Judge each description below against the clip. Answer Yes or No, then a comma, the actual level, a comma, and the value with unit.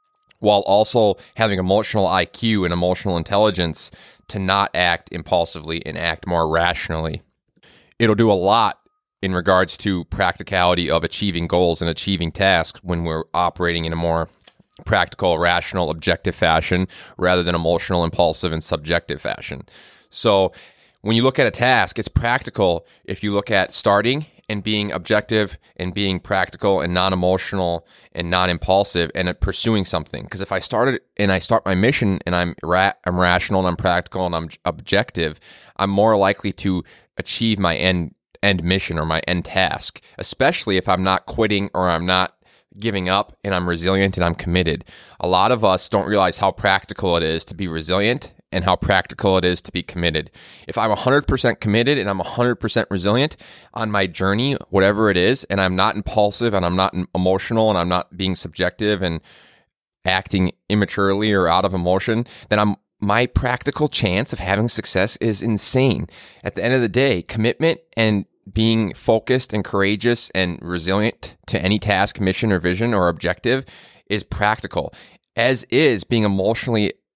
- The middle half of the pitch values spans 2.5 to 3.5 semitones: Yes, average, 3.2 semitones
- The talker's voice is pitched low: Yes, very low, 95 Hz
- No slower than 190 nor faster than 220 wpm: No, average, 165 wpm